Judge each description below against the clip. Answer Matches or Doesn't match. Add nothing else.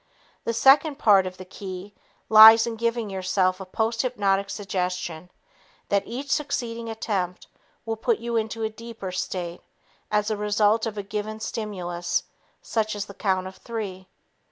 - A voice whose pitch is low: Doesn't match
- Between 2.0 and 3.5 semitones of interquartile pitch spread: Matches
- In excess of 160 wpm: Doesn't match